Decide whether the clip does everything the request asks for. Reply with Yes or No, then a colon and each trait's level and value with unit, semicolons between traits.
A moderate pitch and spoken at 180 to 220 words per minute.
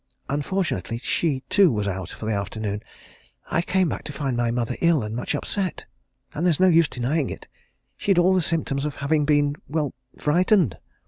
Yes: medium, 145 Hz; average, 185 wpm